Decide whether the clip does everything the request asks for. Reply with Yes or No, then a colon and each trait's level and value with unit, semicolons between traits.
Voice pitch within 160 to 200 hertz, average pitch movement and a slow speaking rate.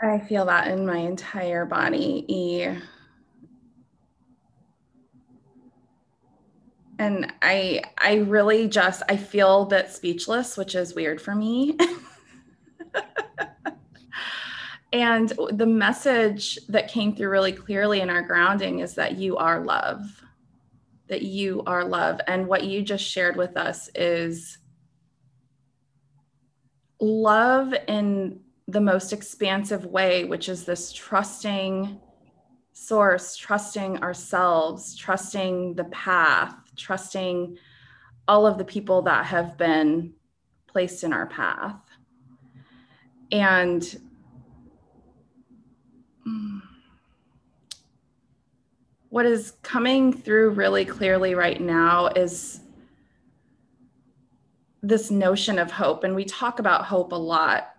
Yes: medium, 185 Hz; average, 4.0 semitones; slow, 100 wpm